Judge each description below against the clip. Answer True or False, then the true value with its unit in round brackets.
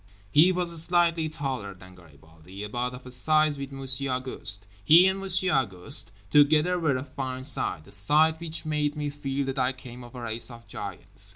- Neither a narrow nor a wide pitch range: True (4.7 semitones)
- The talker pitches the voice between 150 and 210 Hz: False (135 Hz)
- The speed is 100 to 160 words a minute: False (190 wpm)